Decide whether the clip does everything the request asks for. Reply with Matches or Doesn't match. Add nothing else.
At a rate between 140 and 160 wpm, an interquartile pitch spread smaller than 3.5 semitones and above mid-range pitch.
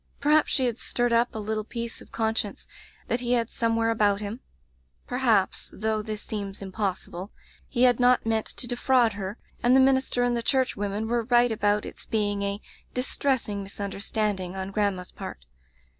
Doesn't match